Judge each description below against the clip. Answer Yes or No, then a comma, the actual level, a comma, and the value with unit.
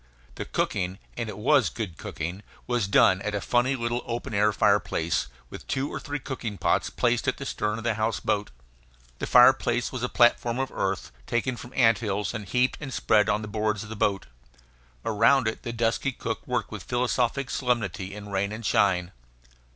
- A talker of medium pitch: No, low, 115 Hz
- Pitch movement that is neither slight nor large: Yes, average, 3.1 semitones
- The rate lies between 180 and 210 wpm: Yes, average, 190 wpm